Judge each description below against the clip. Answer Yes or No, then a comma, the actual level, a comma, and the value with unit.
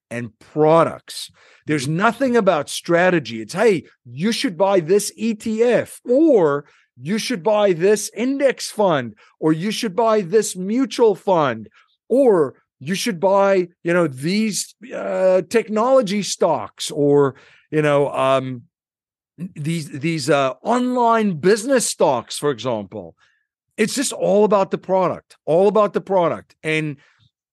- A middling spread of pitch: No, wide, 6.3 semitones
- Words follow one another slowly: Yes, slow, 130 wpm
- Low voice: No, high, 190 Hz